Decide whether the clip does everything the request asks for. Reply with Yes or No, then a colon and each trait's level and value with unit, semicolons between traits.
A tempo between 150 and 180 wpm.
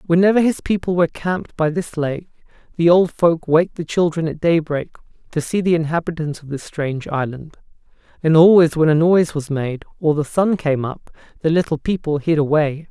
No: average, 190 wpm